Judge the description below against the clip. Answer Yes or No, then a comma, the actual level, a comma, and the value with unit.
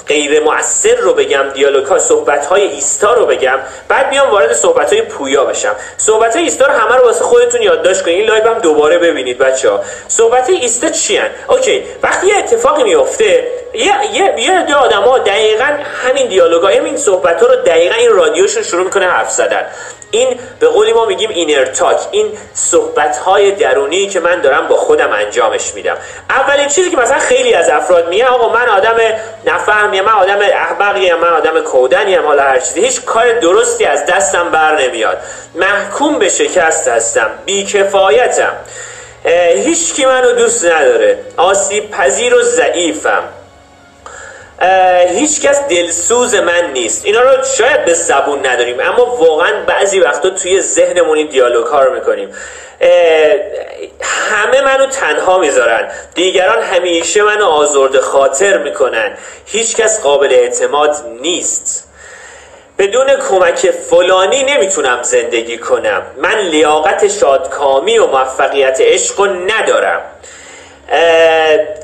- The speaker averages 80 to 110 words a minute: No, average, 145 wpm